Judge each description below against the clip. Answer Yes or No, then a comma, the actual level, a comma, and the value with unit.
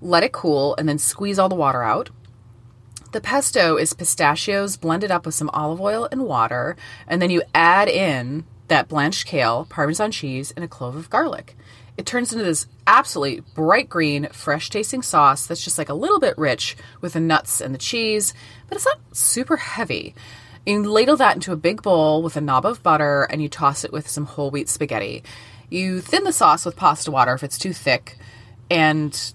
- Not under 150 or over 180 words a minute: No, average, 200 wpm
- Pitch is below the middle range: No, medium, 155 Hz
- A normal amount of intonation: No, wide, 6.0 semitones